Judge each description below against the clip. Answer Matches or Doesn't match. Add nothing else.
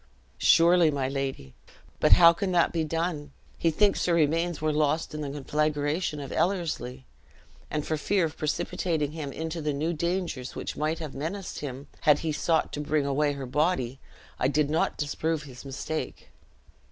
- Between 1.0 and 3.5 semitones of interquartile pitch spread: Matches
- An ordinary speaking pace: Matches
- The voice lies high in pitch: Doesn't match